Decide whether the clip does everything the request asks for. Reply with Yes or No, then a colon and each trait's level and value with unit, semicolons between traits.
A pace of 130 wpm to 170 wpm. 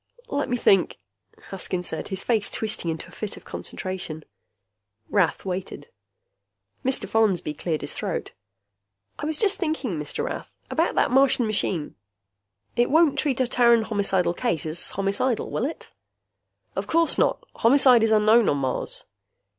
Yes: average, 150 wpm